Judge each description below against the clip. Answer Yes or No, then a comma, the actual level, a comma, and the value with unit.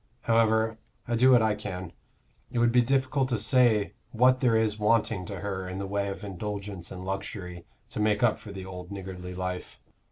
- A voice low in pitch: Yes, low, 105 Hz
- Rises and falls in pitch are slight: No, average, 3.4 semitones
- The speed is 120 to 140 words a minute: No, average, 195 wpm